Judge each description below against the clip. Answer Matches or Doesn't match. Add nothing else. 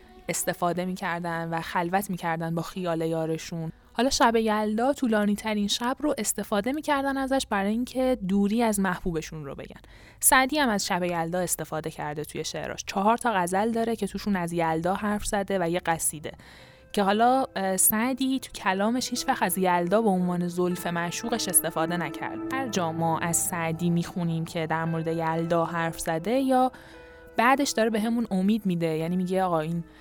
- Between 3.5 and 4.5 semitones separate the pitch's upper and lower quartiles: Doesn't match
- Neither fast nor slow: Doesn't match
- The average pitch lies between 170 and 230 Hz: Matches